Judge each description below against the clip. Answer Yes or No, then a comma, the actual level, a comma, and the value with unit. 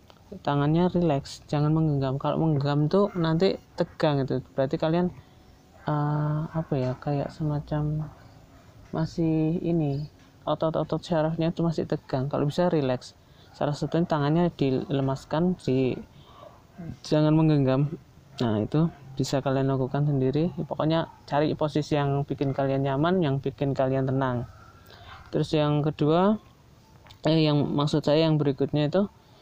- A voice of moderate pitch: Yes, medium, 150 Hz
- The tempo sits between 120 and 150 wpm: Yes, average, 125 wpm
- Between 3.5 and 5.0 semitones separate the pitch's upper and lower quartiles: No, average, 2.9 semitones